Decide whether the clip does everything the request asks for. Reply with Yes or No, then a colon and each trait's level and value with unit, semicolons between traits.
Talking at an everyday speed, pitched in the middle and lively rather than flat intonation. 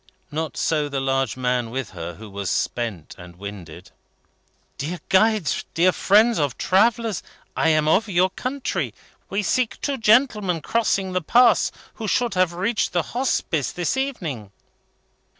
Yes: average, 150 wpm; medium, 175 Hz; wide, 8.8 semitones